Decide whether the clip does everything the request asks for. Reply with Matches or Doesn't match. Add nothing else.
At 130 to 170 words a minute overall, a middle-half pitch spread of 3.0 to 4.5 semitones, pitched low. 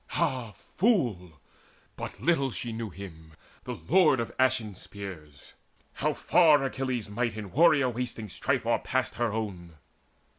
Doesn't match